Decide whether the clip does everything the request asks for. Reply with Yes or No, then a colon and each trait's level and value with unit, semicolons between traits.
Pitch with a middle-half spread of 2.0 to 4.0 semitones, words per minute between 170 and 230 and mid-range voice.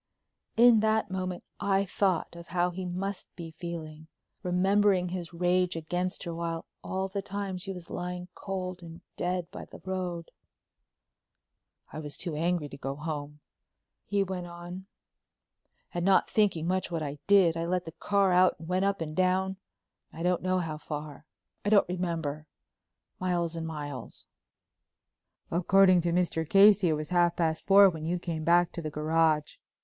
No: narrow, 2.4 semitones; average, 160 wpm; medium, 175 Hz